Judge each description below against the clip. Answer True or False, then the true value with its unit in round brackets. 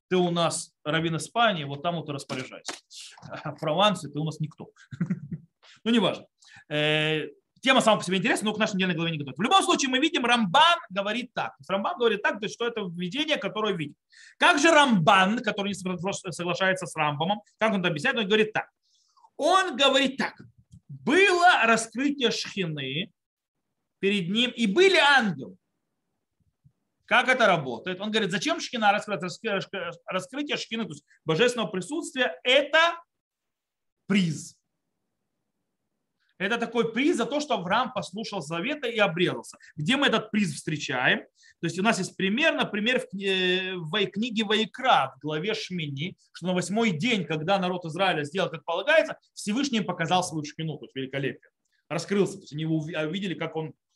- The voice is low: False (200 Hz)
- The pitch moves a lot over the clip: True (5.9 semitones)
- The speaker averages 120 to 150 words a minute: False (160 wpm)